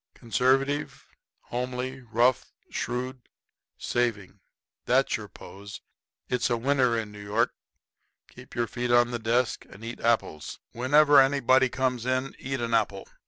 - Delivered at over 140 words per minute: No, slow, 135 wpm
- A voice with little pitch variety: Yes, narrow, 2.1 semitones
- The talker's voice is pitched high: No, low, 120 Hz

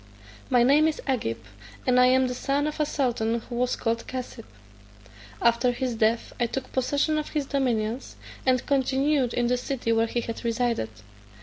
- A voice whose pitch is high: Yes, very high, 250 Hz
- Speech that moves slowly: No, average, 180 wpm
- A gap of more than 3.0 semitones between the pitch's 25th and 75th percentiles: No, narrow, 2.6 semitones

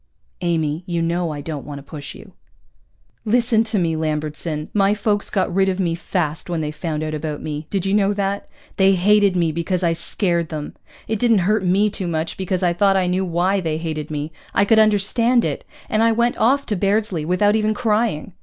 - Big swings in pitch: No, average, 4.4 semitones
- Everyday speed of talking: No, fast, 215 wpm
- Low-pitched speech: No, medium, 185 Hz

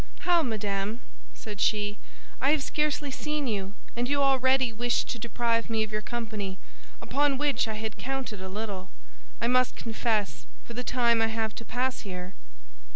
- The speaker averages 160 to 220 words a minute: Yes, average, 170 wpm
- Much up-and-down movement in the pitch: No, average, 3.6 semitones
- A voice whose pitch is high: Yes, high, 230 Hz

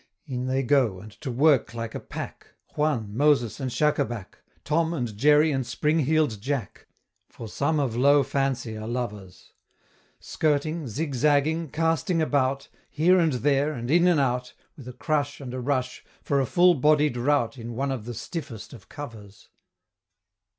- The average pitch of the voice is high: No, low, 135 Hz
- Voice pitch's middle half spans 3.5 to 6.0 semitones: Yes, average, 4.0 semitones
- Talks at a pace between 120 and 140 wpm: No, average, 160 wpm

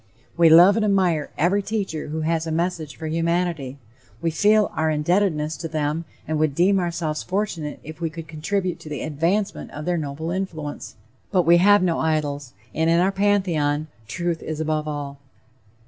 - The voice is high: No, medium, 165 Hz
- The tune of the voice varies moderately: Yes, average, 3.0 semitones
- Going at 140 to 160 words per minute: No, average, 180 wpm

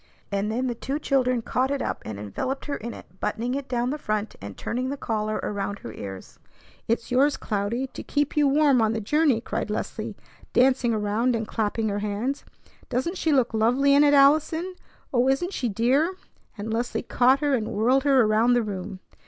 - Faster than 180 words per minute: Yes, average, 200 wpm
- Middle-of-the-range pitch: No, high, 245 Hz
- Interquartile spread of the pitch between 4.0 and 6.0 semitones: Yes, average, 4.3 semitones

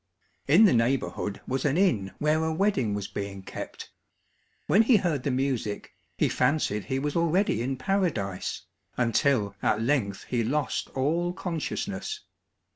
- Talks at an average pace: Yes, average, 145 wpm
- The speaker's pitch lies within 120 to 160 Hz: Yes, low, 135 Hz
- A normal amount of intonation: No, wide, 7.1 semitones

